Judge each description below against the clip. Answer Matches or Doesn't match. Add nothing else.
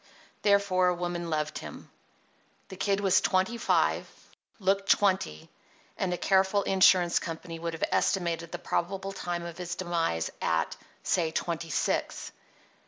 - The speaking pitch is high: Doesn't match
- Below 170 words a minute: Matches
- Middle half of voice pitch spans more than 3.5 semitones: Doesn't match